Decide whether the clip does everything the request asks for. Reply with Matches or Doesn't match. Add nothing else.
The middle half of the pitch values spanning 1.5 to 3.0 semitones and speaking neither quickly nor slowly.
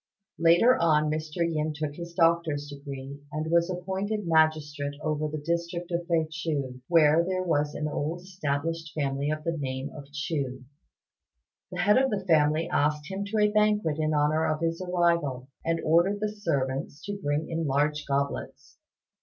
Matches